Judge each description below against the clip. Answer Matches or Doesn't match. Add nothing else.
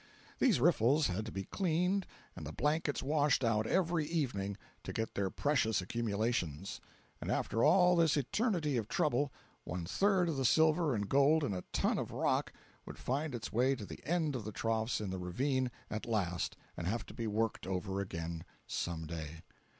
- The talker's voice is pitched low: Matches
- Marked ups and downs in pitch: Matches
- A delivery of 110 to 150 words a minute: Doesn't match